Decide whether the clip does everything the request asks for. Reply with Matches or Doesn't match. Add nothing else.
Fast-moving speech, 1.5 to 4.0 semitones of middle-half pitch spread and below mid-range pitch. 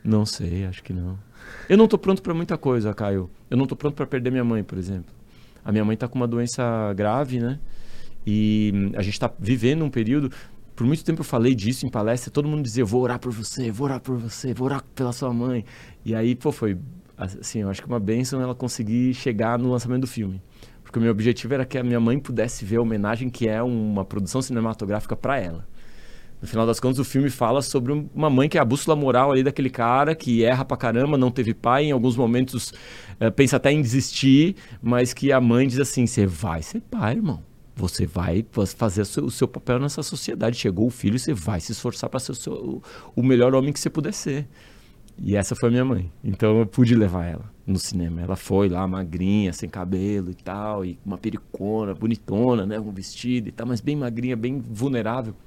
Matches